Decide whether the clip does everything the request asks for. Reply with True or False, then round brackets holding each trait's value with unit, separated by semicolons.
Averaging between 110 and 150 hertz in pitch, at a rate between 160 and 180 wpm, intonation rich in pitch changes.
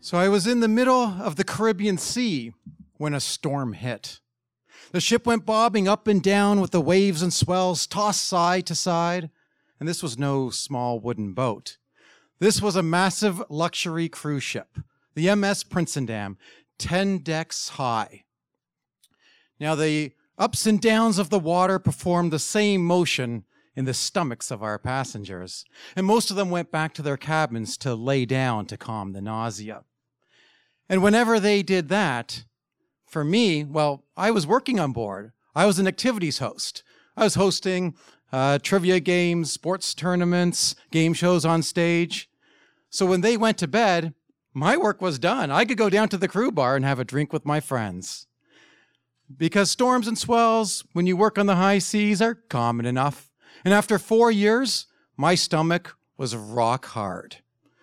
False (175 Hz; 170 wpm; 6.6 semitones)